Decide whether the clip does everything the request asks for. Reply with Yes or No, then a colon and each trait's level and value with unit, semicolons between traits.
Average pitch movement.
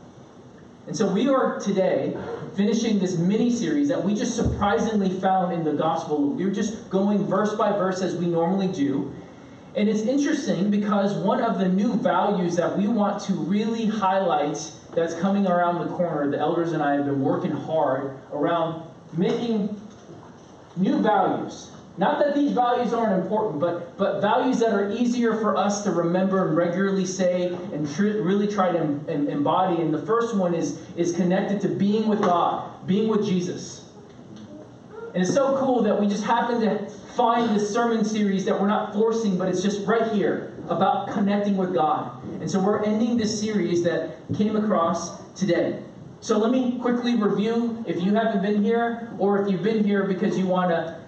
Yes: average, 3.9 semitones